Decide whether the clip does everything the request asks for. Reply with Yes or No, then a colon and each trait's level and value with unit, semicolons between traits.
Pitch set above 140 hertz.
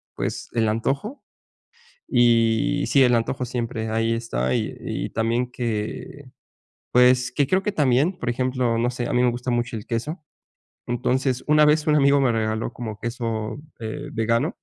No: low, 120 Hz